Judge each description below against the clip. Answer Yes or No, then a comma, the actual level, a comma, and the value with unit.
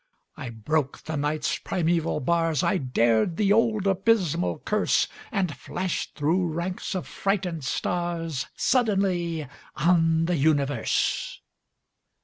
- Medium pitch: Yes, medium, 165 Hz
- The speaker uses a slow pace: Yes, slow, 115 wpm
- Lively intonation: No, average, 3.9 semitones